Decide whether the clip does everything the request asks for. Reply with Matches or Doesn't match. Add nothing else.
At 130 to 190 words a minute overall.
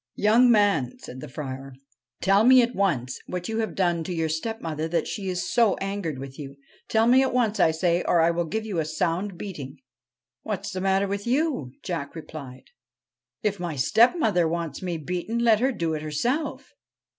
Doesn't match